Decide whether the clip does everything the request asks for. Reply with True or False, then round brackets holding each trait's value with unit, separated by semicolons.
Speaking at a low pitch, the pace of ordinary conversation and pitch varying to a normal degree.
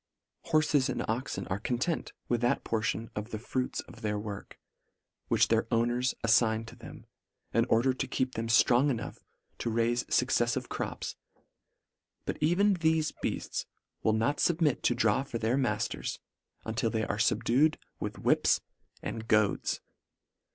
True (120 Hz; 150 wpm; 3.0 semitones)